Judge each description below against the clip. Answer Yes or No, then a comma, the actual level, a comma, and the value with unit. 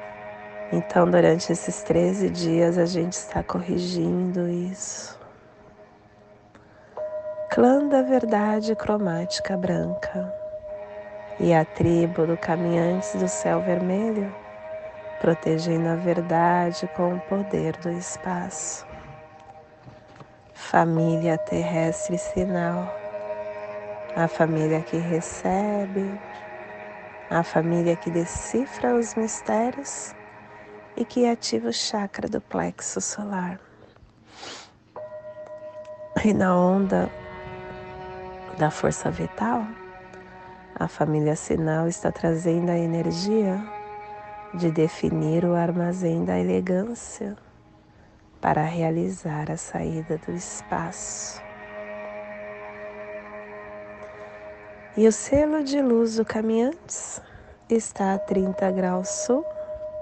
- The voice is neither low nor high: Yes, medium, 170 Hz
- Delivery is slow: Yes, slow, 90 wpm